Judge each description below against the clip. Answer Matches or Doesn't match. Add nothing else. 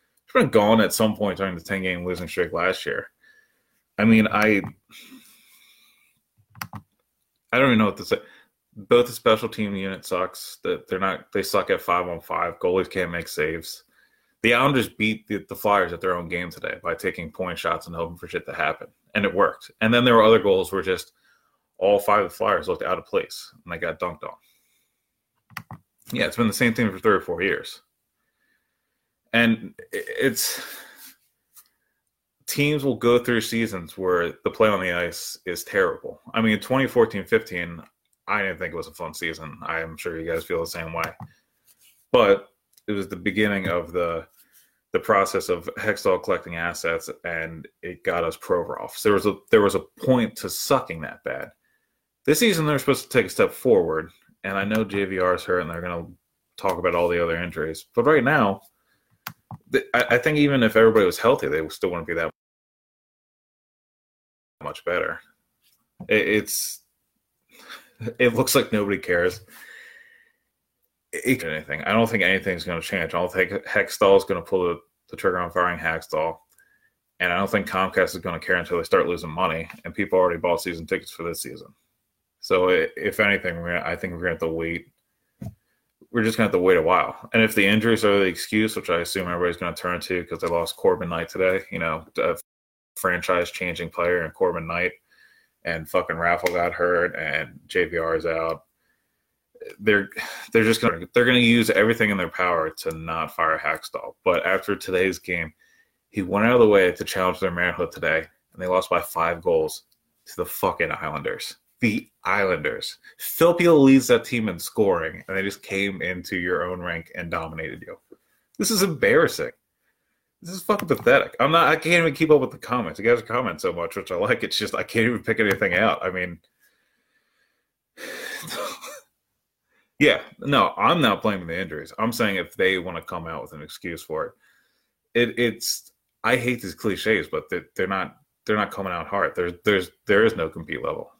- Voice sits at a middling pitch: Doesn't match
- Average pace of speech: Matches